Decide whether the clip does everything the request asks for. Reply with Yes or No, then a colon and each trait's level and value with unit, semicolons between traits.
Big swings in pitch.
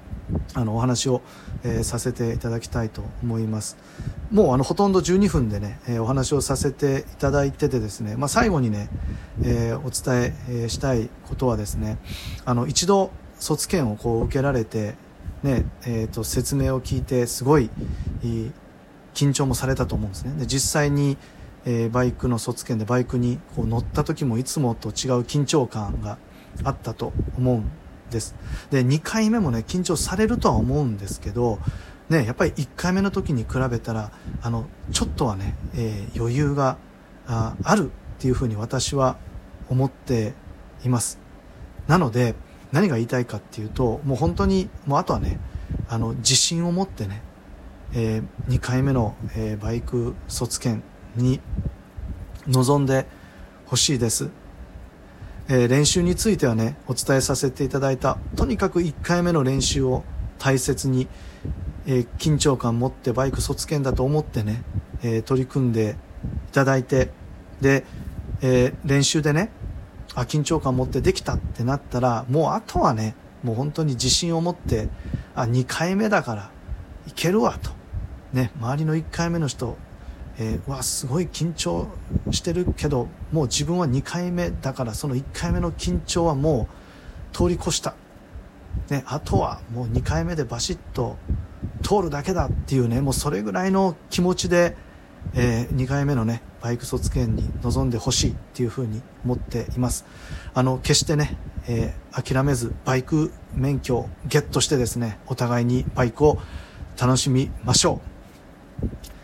No: average, 4.4 semitones